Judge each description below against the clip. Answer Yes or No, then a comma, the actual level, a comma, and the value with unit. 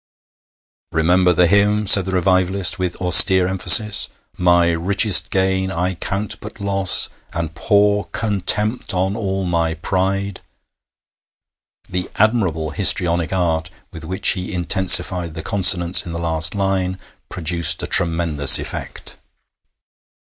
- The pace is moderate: No, slow, 120 wpm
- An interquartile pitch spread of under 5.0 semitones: Yes, narrow, 2.4 semitones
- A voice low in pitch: Yes, very low, 90 Hz